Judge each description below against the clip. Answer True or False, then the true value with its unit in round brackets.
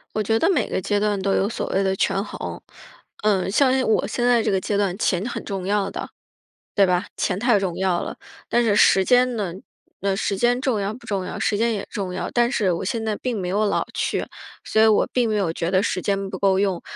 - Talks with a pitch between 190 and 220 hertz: True (205 Hz)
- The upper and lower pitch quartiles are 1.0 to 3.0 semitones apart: True (2.7 semitones)